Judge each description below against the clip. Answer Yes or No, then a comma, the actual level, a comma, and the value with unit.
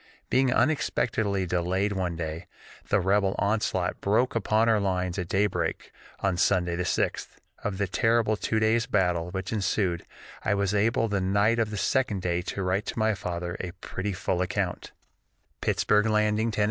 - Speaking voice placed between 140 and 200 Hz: No, low, 100 Hz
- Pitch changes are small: No, average, 3.1 semitones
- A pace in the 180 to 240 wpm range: No, average, 170 wpm